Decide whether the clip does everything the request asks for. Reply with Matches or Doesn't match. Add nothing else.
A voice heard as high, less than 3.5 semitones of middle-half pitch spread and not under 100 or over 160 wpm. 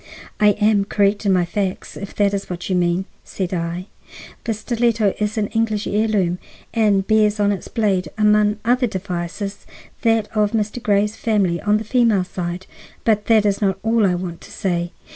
Doesn't match